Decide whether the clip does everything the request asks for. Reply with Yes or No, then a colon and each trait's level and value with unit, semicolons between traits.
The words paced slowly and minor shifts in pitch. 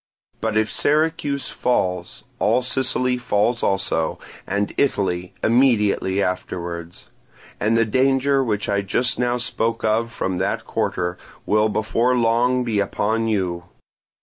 No: slow, 125 wpm; average, 4.3 semitones